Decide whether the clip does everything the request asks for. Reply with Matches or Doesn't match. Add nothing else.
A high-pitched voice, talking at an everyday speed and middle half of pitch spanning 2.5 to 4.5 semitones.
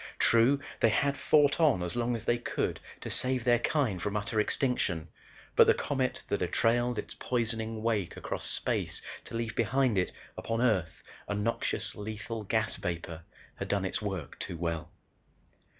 Doesn't match